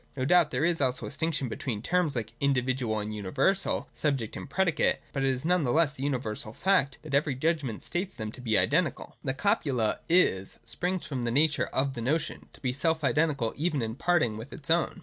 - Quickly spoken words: Yes, fast, 215 wpm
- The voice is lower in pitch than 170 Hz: Yes, medium, 140 Hz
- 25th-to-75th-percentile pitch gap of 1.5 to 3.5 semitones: No, average, 4.8 semitones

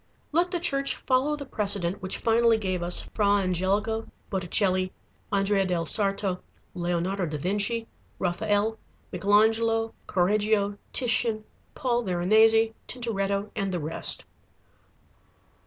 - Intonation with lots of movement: No, average, 3.3 semitones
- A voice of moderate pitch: No, high, 205 Hz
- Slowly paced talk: Yes, slow, 110 wpm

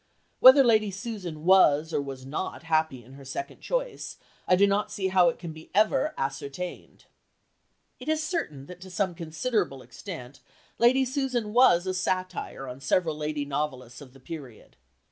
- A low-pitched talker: No, medium, 175 Hz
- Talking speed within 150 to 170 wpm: Yes, average, 165 wpm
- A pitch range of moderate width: No, wide, 7.0 semitones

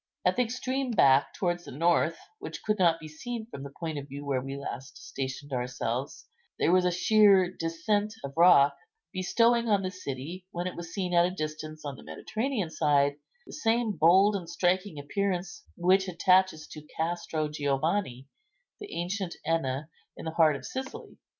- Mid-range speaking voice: Yes, medium, 175 Hz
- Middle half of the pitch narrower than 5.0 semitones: No, average, 5.3 semitones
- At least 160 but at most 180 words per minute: Yes, average, 175 wpm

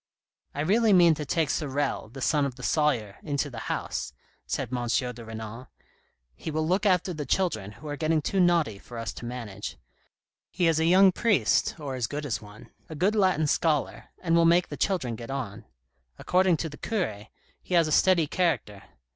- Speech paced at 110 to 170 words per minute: No, fast, 205 wpm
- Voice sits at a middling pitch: Yes, medium, 150 Hz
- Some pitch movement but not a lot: No, wide, 6.1 semitones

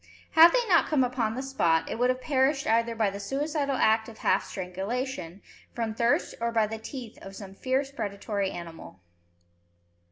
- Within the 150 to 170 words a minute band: No, average, 180 wpm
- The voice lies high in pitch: Yes, high, 230 Hz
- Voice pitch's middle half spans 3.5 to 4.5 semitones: No, average, 5.1 semitones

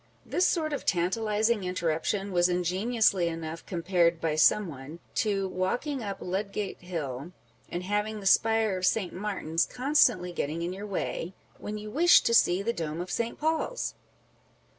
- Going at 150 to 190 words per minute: Yes, average, 160 wpm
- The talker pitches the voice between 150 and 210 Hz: Yes, high, 190 Hz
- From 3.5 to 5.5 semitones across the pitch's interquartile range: Yes, average, 4.0 semitones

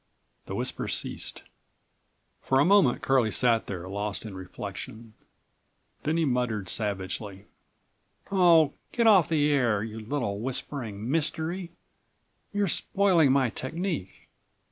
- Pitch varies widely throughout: Yes, wide, 7.3 semitones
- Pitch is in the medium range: No, low, 130 Hz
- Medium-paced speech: No, slow, 120 wpm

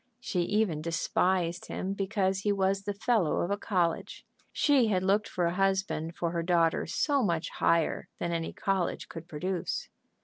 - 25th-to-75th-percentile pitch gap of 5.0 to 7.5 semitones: No, average, 2.9 semitones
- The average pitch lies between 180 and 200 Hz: Yes, medium, 185 Hz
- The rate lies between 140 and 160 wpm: No, average, 170 wpm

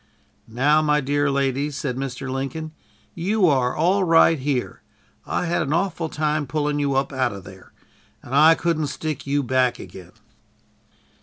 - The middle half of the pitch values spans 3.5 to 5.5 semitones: No, average, 3.0 semitones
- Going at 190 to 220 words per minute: No, average, 160 wpm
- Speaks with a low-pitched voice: No, medium, 145 Hz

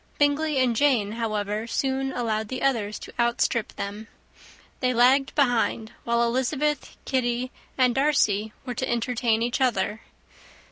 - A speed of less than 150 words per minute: Yes, slow, 135 wpm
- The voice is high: Yes, high, 240 Hz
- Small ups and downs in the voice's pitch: No, average, 3.2 semitones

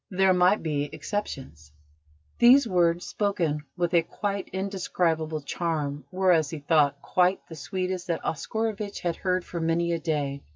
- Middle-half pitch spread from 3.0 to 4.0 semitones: Yes, average, 3.4 semitones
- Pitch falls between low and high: Yes, medium, 170 Hz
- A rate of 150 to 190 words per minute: Yes, average, 155 wpm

